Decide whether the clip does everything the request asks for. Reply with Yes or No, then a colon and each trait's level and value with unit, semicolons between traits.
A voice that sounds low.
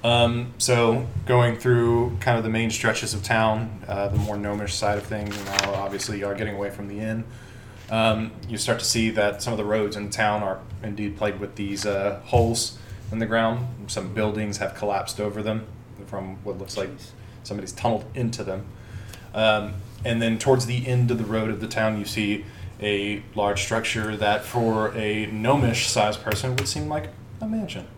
Yes: low, 110 Hz